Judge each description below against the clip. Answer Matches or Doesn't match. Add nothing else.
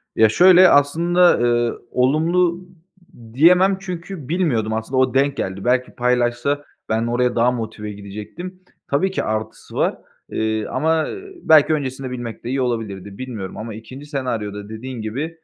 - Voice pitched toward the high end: Doesn't match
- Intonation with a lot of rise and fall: Matches